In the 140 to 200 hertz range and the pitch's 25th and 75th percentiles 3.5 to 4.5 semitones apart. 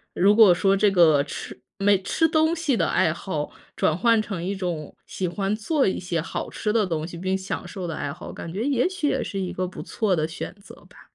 Yes: high, 190 Hz; average, 4.2 semitones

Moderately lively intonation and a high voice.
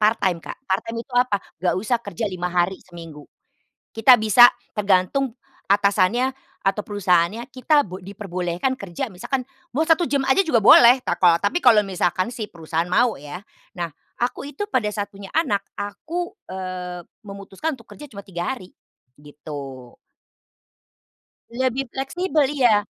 No: wide, 5.8 semitones; high, 205 Hz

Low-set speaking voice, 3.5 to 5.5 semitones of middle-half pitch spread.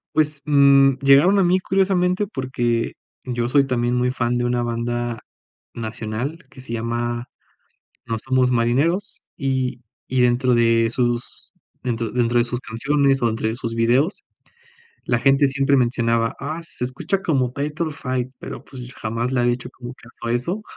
No: low, 125 Hz; average, 2.7 semitones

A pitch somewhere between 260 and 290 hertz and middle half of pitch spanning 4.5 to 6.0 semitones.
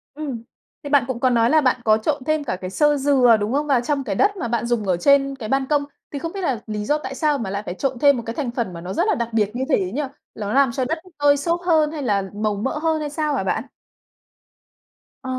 Yes: very high, 265 Hz; average, 4.9 semitones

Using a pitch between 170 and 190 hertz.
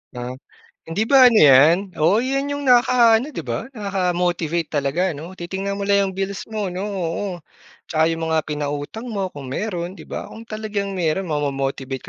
Yes: medium, 185 Hz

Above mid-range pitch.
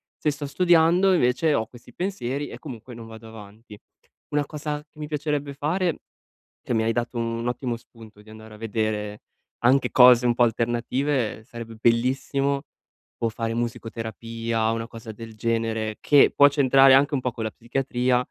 No: low, 120 Hz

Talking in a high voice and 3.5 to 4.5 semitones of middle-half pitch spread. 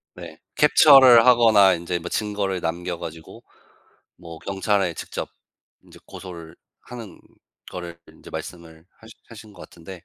No: very low, 90 Hz; average, 4.2 semitones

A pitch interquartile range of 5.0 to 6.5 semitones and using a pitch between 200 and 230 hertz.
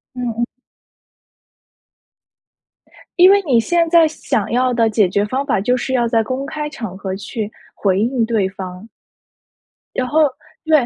No: average, 5.3 semitones; high, 240 Hz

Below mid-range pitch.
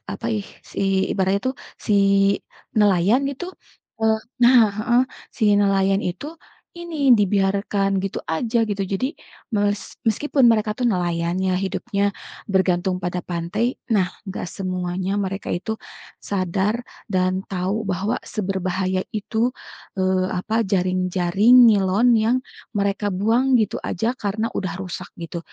No: high, 195 Hz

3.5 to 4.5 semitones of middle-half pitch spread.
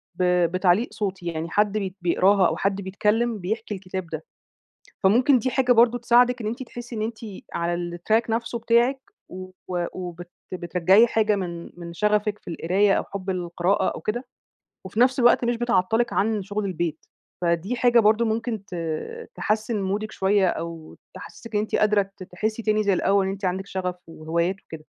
Yes: average, 3.8 semitones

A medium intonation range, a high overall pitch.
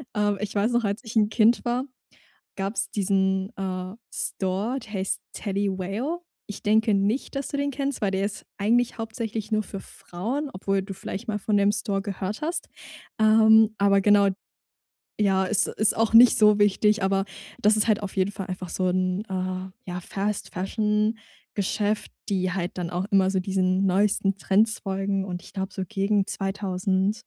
No: narrow, 2.1 semitones; high, 200 Hz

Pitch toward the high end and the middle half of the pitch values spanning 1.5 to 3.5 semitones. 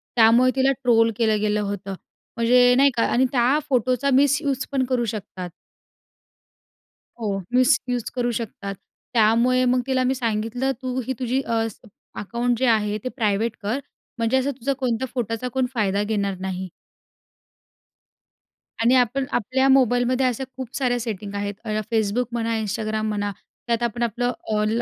Yes: high, 235 Hz; average, 3.0 semitones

